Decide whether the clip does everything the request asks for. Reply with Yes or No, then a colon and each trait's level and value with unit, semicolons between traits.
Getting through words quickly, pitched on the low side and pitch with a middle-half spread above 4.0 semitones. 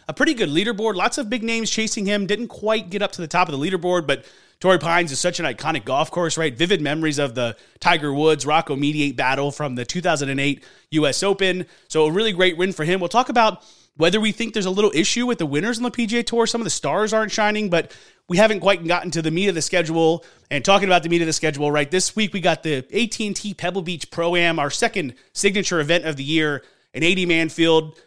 No: fast, 245 wpm; medium, 175 Hz; average, 4.7 semitones